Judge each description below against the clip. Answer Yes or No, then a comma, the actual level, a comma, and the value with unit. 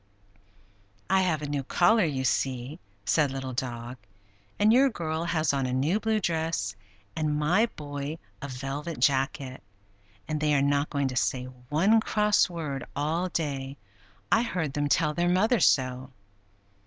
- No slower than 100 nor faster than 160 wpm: Yes, average, 155 wpm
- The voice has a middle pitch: Yes, medium, 150 Hz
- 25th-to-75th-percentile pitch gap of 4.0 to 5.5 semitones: Yes, average, 4.3 semitones